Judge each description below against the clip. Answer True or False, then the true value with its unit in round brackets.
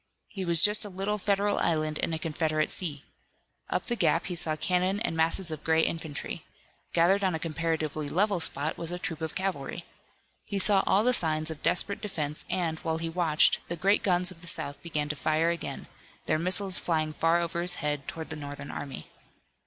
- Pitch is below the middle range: False (165 Hz)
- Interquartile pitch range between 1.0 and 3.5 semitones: True (3.1 semitones)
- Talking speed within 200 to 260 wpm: True (205 wpm)